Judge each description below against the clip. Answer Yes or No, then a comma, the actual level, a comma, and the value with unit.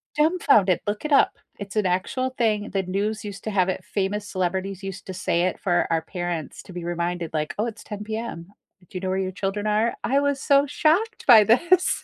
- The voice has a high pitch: Yes, high, 200 Hz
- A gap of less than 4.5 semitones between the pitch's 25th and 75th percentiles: Yes, average, 3.7 semitones